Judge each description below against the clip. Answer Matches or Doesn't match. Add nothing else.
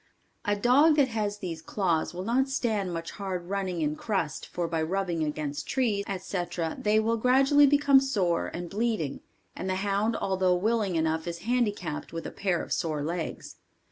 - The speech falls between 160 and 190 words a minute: Matches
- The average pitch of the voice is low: Doesn't match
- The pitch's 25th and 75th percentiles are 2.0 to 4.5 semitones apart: Doesn't match